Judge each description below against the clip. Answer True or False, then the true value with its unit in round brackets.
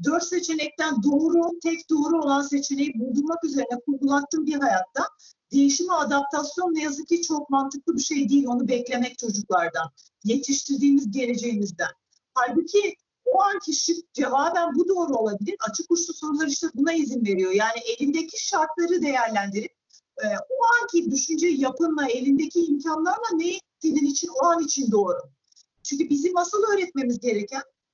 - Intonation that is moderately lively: True (4.5 semitones)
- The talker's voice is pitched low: False (290 Hz)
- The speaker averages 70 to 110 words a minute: False (135 wpm)